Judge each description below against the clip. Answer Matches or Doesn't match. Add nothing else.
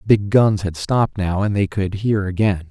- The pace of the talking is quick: Matches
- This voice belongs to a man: Matches